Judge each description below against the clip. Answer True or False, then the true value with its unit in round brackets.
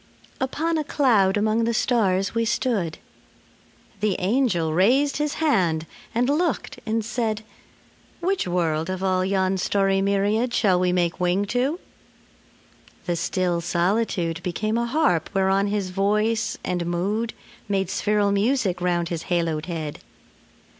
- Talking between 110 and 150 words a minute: True (135 wpm)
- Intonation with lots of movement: False (4.4 semitones)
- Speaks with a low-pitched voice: False (200 Hz)